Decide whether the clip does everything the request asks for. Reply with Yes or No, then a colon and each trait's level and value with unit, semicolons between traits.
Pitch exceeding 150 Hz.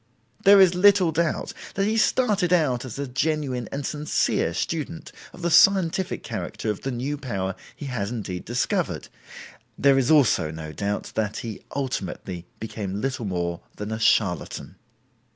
No: low, 130 Hz